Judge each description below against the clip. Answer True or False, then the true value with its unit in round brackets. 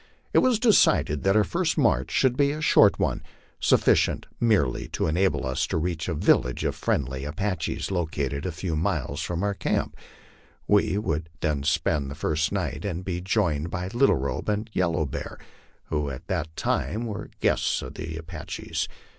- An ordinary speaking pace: True (180 wpm)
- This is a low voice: True (85 Hz)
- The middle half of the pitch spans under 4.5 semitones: False (4.9 semitones)